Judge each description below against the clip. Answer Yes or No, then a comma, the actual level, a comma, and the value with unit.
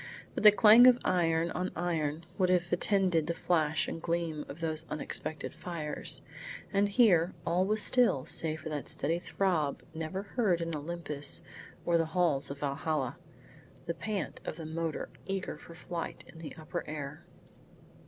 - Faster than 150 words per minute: Yes, average, 165 wpm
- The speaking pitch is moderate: Yes, medium, 165 Hz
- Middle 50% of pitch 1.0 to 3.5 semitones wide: Yes, average, 2.7 semitones